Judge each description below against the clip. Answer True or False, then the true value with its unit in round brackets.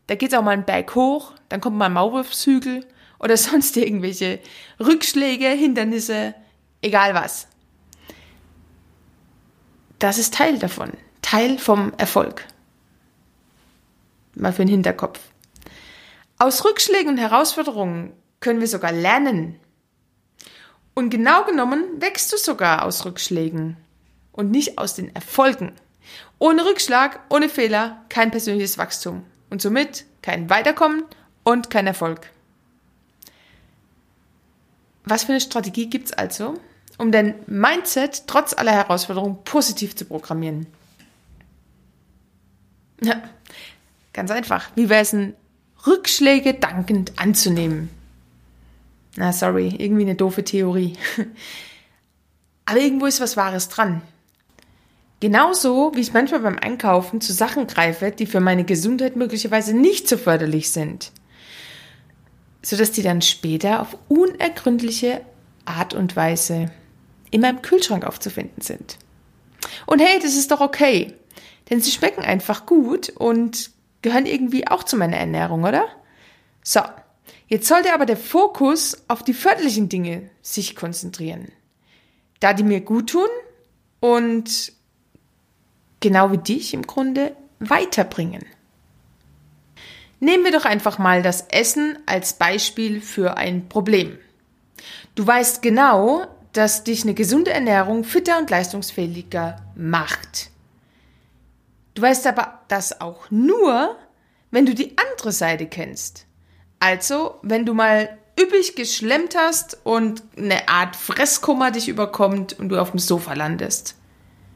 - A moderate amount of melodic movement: False (6.6 semitones)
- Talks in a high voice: True (220 Hz)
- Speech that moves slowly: True (120 wpm)